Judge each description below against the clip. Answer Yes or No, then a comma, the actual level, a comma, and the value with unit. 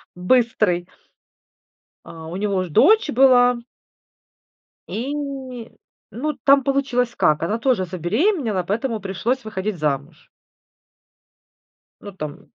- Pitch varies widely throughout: Yes, wide, 6.3 semitones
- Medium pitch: No, high, 215 Hz